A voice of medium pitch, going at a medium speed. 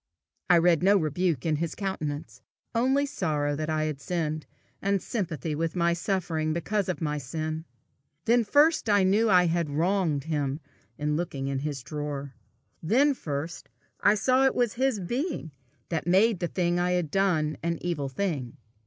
Yes: medium, 170 Hz; average, 170 wpm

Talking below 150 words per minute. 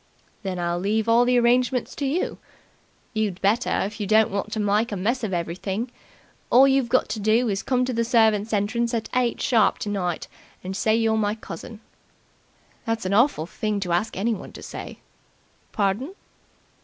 No: average, 180 wpm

